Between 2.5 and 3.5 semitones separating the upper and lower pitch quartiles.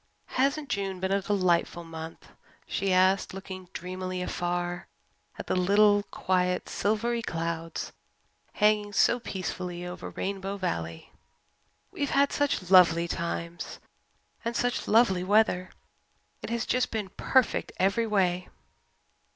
Yes: average, 3.0 semitones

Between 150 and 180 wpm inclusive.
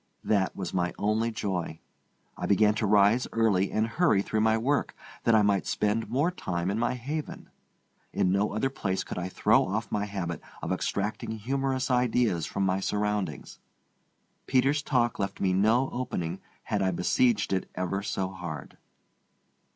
Yes: average, 165 wpm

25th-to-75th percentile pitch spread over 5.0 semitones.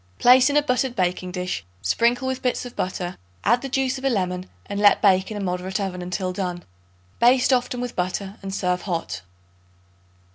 Yes: wide, 5.4 semitones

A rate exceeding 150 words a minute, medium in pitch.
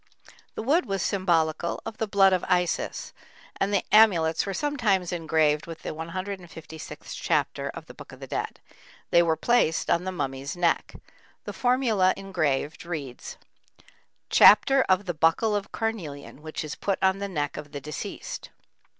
Yes: average, 160 wpm; medium, 180 Hz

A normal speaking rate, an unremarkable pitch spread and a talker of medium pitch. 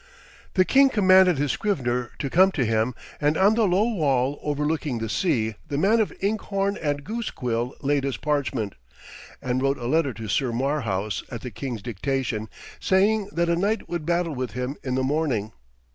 No: average, 180 wpm; wide, 6.9 semitones; medium, 145 Hz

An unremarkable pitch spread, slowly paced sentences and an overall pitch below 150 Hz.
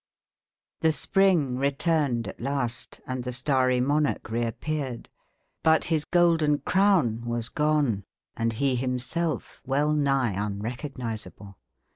Yes: average, 4.3 semitones; slow, 110 wpm; low, 135 Hz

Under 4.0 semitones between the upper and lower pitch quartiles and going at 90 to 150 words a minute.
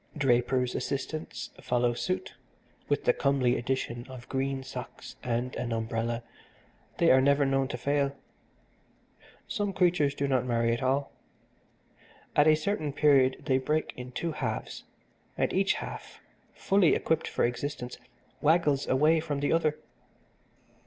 Yes: average, 3.4 semitones; average, 140 wpm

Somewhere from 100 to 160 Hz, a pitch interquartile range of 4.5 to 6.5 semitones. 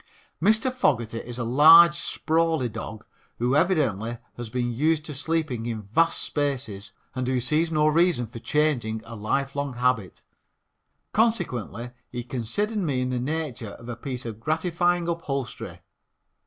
Yes: low, 135 Hz; wide, 5.5 semitones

